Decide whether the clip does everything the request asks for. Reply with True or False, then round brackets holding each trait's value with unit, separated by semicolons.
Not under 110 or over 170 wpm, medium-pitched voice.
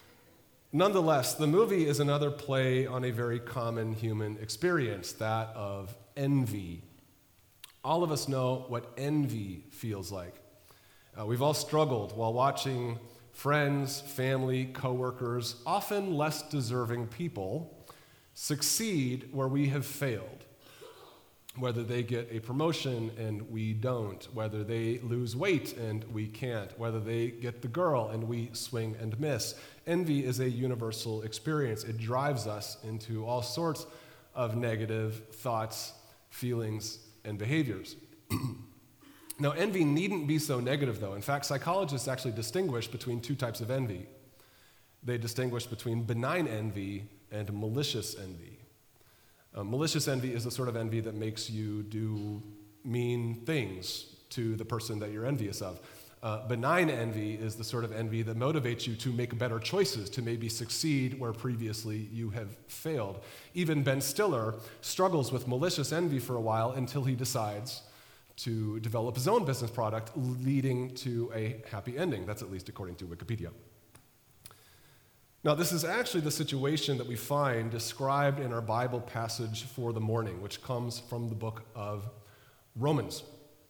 False (150 wpm; 120 Hz)